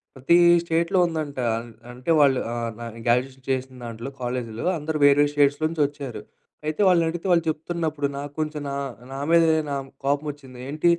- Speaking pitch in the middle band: Yes, medium, 145 Hz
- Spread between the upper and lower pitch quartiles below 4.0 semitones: Yes, average, 3.3 semitones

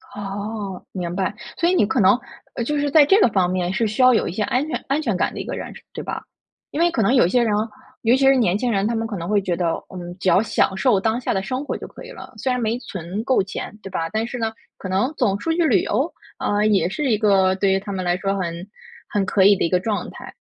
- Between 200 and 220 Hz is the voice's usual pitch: Yes, high, 210 Hz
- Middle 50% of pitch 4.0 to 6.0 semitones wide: Yes, average, 4.6 semitones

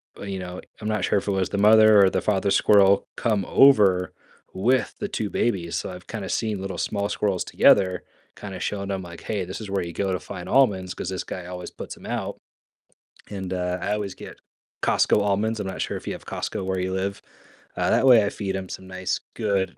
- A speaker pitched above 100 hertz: No, very low, 95 Hz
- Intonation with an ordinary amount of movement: No, narrow, 2.0 semitones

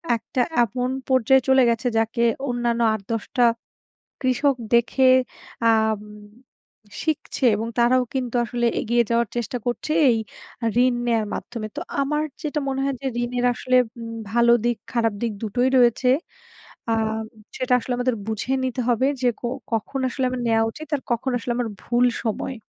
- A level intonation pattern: Yes, narrow, 2.0 semitones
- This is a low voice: No, high, 240 Hz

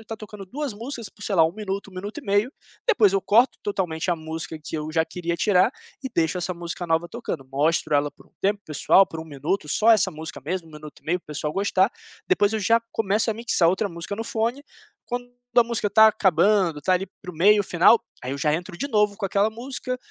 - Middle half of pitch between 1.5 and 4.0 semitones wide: No, average, 4.8 semitones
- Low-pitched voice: No, high, 195 Hz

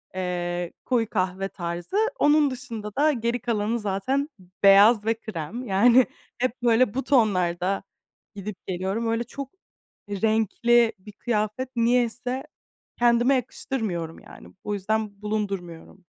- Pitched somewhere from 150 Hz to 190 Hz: No, high, 220 Hz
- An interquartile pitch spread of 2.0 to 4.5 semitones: Yes, average, 3.9 semitones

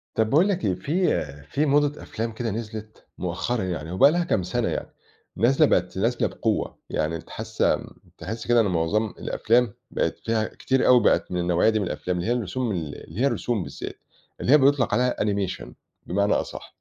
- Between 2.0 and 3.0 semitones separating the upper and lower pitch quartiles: No, average, 5.2 semitones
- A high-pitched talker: No, low, 110 Hz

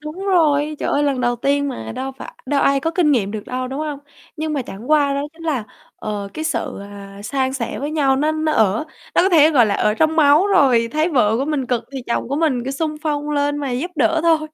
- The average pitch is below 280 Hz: No, very high, 285 Hz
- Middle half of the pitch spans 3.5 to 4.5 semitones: Yes, average, 4.0 semitones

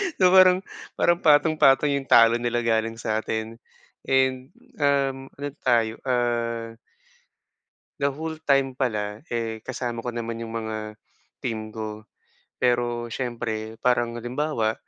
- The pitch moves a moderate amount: Yes, average, 3.0 semitones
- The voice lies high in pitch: No, low, 120 Hz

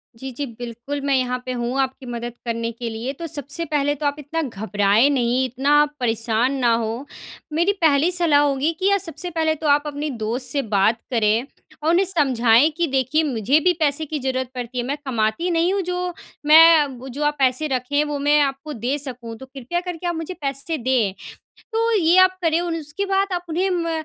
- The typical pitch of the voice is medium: No, very high, 280 Hz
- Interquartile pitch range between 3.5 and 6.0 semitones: Yes, average, 4.7 semitones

